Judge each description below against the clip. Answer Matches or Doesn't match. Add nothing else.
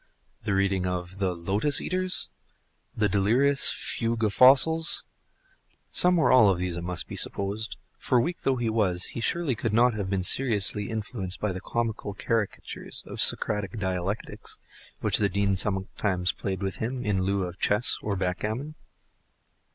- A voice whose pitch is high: Doesn't match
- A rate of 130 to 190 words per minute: Matches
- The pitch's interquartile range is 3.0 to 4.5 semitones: Matches